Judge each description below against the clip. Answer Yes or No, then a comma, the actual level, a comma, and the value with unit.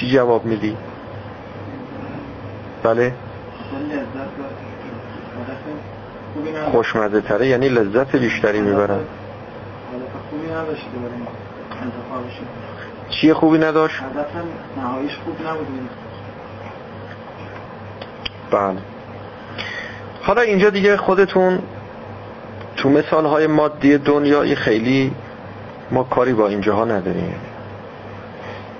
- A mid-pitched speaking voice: No, low, 125 Hz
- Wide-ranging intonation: Yes, wide, 5.7 semitones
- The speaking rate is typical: No, slow, 65 wpm